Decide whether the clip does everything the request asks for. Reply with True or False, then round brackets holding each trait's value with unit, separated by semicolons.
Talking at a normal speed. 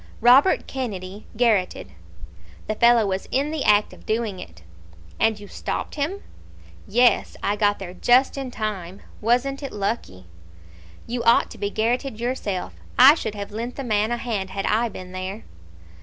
True (165 wpm)